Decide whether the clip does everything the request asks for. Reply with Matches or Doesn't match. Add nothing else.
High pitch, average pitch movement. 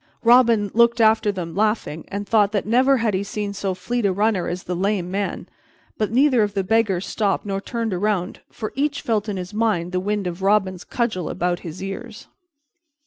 Matches